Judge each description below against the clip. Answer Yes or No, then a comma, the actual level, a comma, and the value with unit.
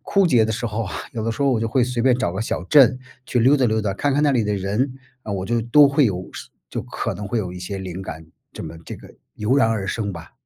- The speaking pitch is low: Yes, low, 110 Hz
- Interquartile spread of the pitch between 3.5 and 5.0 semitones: Yes, average, 4.5 semitones